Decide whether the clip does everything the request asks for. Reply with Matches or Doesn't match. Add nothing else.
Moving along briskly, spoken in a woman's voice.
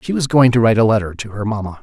Doesn't match